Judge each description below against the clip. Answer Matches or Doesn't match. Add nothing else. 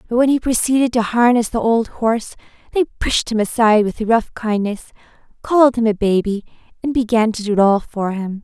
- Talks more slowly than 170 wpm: Doesn't match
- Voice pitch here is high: Matches